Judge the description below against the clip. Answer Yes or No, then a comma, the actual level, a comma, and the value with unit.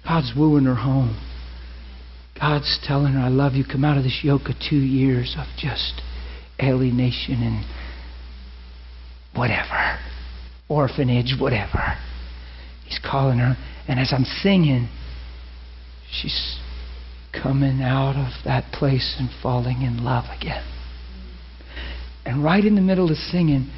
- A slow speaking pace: Yes, slow, 125 wpm